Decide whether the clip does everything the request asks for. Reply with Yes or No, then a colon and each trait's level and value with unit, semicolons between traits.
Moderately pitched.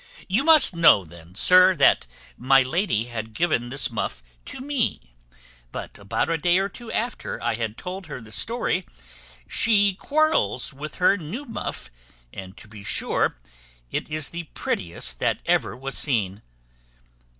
Yes: medium, 150 Hz